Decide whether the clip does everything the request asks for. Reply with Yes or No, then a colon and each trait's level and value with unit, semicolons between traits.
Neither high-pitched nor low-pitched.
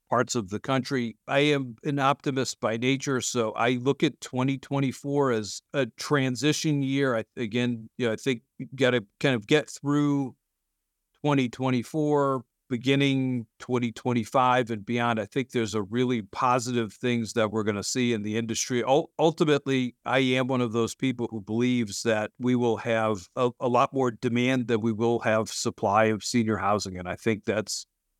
No: low, 125 Hz